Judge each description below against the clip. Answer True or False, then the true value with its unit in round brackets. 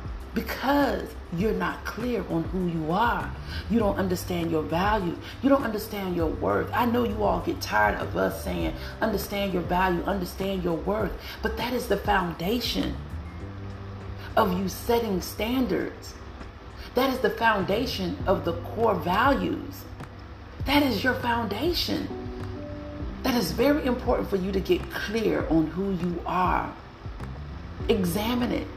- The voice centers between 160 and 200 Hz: True (185 Hz)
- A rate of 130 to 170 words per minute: True (145 wpm)